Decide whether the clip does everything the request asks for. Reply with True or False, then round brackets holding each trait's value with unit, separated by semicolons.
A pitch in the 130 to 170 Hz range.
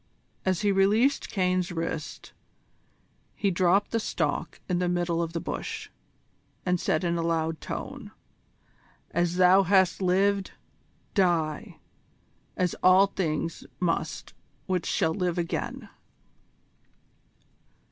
False (180 Hz)